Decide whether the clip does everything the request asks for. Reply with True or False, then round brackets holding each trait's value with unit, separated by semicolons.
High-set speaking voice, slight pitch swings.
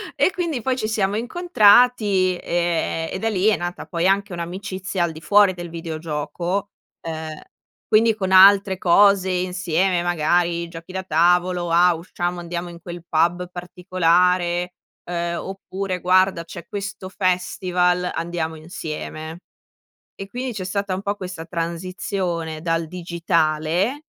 False (180 Hz; 2.3 semitones)